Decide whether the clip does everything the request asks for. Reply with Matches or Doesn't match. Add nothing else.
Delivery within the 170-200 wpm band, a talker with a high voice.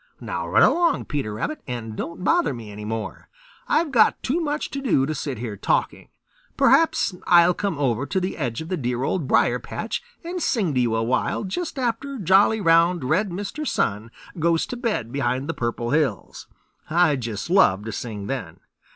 Doesn't match